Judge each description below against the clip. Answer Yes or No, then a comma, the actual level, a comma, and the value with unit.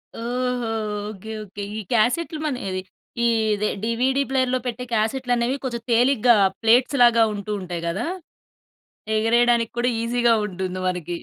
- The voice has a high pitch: Yes, high, 235 Hz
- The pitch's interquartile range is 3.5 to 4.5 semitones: No, average, 2.7 semitones